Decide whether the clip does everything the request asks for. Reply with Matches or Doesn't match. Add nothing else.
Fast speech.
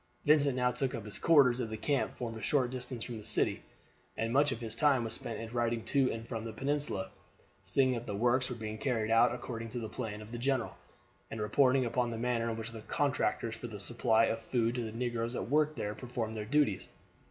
Matches